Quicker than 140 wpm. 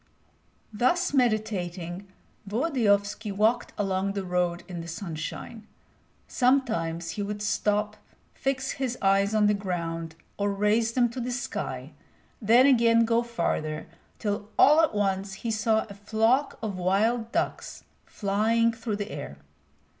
No: slow, 135 wpm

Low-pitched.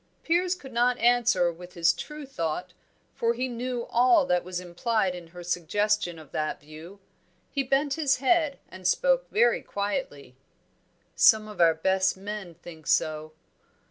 No: high, 205 Hz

